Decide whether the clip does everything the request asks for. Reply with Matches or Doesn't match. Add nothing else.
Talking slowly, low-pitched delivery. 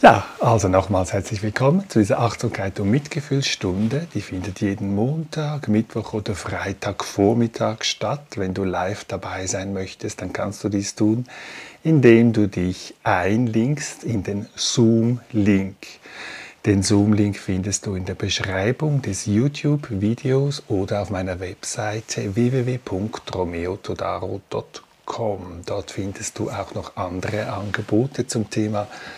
Matches